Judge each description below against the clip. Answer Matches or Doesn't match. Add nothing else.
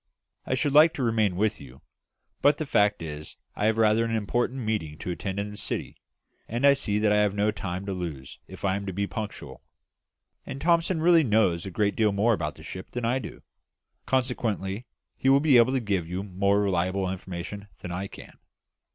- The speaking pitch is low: Matches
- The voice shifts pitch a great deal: Doesn't match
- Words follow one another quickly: Matches